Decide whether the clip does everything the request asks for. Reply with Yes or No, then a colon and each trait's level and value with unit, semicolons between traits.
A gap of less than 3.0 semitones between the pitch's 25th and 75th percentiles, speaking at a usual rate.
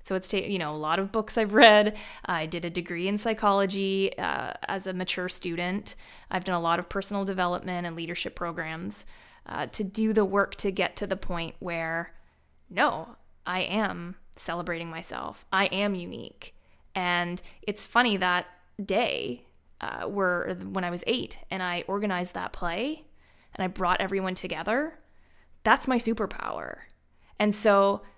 Yes: narrow, 2.6 semitones; average, 165 wpm